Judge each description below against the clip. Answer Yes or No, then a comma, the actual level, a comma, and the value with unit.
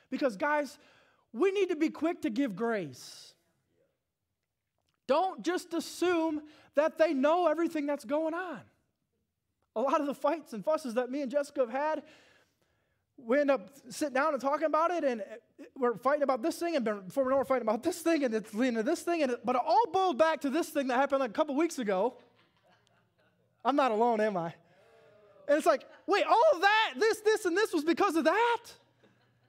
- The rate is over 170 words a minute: Yes, fast, 205 wpm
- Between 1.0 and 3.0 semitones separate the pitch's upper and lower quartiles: No, average, 4.1 semitones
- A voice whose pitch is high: Yes, very high, 295 Hz